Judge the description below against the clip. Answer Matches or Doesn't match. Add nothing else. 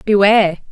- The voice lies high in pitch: Matches